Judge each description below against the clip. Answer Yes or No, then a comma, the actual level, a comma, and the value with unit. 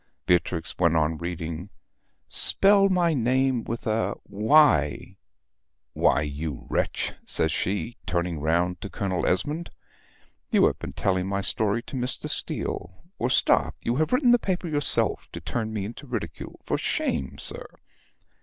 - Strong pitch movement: Yes, wide, 7.5 semitones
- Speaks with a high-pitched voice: No, low, 105 Hz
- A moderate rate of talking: Yes, average, 145 wpm